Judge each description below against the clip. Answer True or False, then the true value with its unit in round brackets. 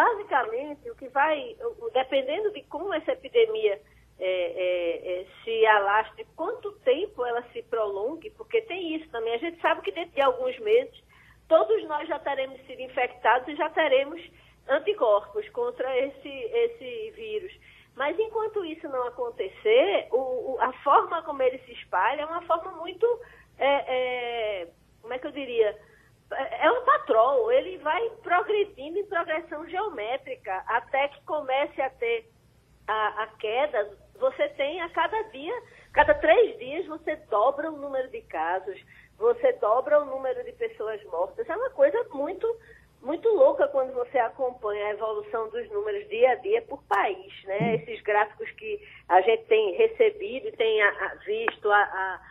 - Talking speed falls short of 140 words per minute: False (155 wpm)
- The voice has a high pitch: True (320 Hz)